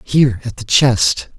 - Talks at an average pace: Yes, average, 175 wpm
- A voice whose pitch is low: Yes, low, 120 Hz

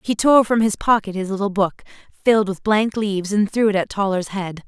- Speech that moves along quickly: Yes, fast, 230 wpm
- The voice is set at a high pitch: Yes, high, 205 Hz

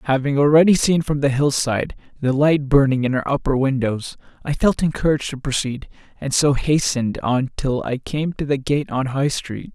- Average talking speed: Yes, average, 190 wpm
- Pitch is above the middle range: No, medium, 140 Hz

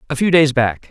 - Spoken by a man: Yes, male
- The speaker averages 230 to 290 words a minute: Yes, fast, 265 wpm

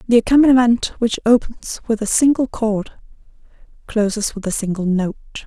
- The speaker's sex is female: Yes, female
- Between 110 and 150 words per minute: Yes, average, 145 wpm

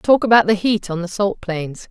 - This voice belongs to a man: No, female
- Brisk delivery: Yes, fast, 250 wpm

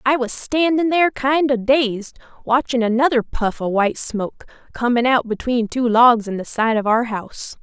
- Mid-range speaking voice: No, high, 245 Hz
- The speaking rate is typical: Yes, average, 190 wpm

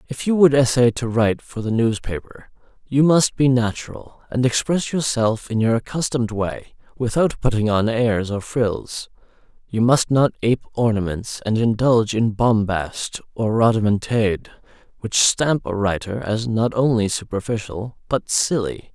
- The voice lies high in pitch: No, low, 115 Hz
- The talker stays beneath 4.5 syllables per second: No, 4.6 syllables/s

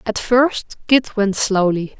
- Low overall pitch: No, high, 215 Hz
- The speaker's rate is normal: Yes, average, 150 wpm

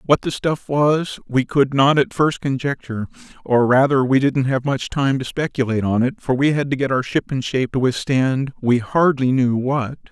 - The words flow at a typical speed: No, fast, 215 wpm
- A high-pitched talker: No, low, 135 Hz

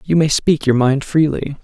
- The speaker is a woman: No, male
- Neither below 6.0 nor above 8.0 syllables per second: No, 4.6 syllables/s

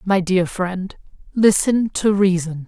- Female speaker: Yes, female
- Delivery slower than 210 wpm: Yes, slow, 135 wpm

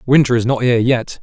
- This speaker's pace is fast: Yes, fast, 245 wpm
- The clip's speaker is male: Yes, male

